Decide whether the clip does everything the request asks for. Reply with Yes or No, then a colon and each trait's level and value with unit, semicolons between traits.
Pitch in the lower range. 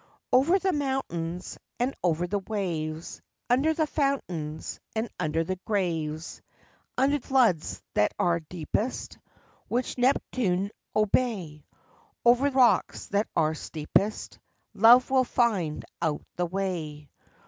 No: high, 195 Hz